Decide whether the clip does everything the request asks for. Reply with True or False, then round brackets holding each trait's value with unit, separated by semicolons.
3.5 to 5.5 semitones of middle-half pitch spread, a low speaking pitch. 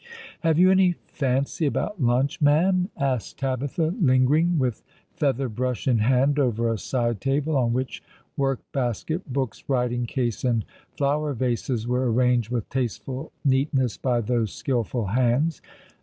False (2.9 semitones; 130 Hz)